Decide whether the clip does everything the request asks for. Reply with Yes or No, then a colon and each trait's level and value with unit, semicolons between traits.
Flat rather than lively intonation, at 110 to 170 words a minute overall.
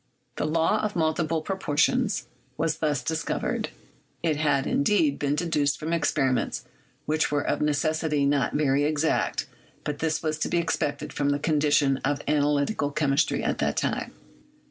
Yes: narrow, 2.0 semitones; average, 155 wpm